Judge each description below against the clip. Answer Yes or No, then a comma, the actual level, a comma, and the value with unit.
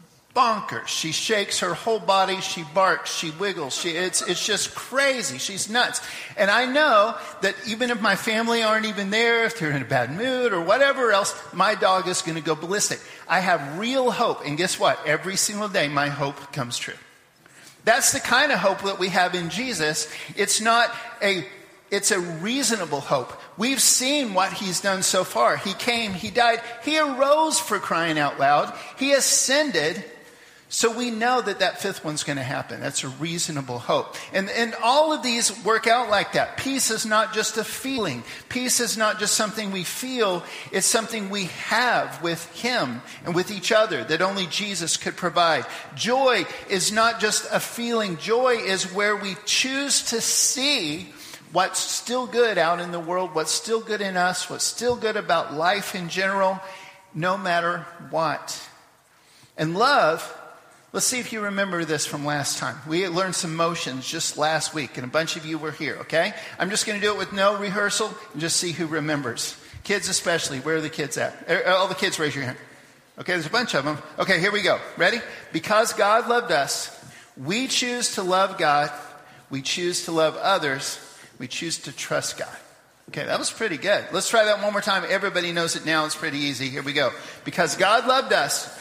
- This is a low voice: No, high, 195 Hz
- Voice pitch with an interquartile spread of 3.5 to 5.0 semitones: No, wide, 5.5 semitones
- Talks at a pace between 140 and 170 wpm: No, average, 195 wpm